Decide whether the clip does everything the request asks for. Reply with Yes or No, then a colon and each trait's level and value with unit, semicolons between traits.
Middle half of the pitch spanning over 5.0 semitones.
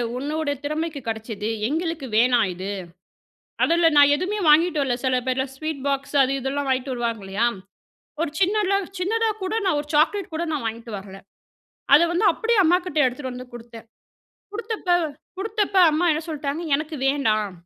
Yes: wide, 5.5 semitones